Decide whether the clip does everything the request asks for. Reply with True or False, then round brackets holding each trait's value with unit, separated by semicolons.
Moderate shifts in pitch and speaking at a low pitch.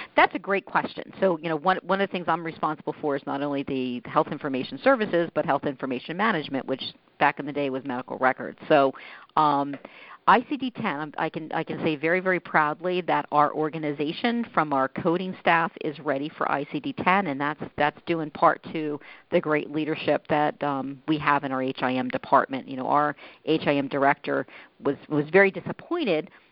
False (3.4 semitones; 155 Hz)